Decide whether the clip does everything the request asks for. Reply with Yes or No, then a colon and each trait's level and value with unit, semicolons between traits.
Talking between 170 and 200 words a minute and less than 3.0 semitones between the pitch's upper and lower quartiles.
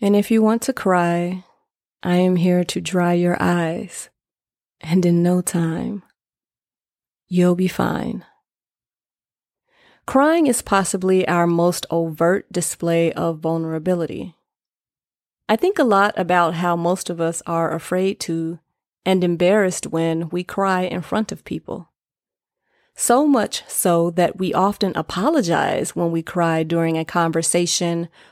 No: slow, 135 wpm; narrow, 2.5 semitones